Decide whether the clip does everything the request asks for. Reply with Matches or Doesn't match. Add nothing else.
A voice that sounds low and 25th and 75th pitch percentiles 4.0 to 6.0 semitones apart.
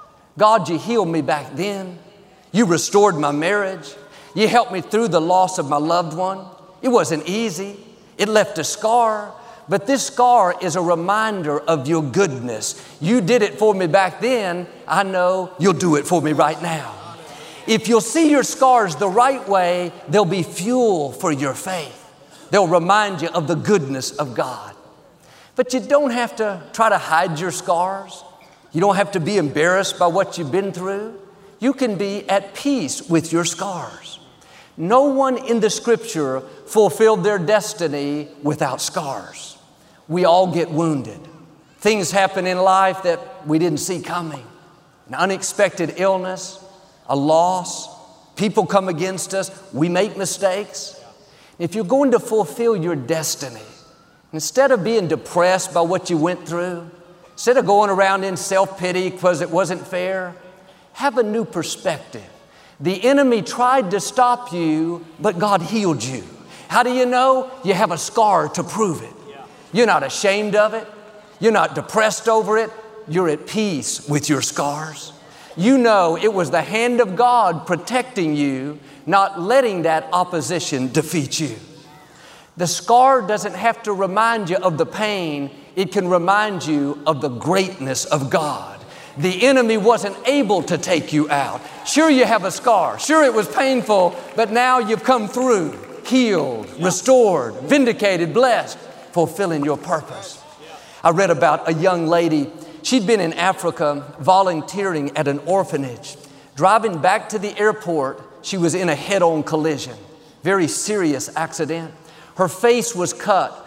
Doesn't match